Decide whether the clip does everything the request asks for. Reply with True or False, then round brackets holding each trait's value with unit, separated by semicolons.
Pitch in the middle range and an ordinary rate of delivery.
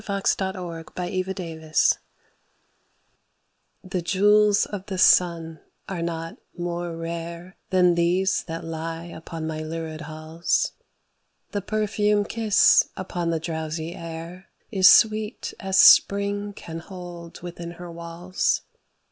False (175 Hz; 115 wpm)